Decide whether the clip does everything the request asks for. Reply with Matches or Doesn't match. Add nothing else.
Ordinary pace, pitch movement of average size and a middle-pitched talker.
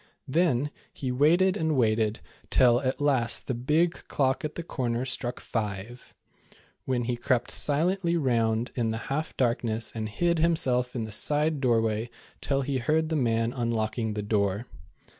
Doesn't match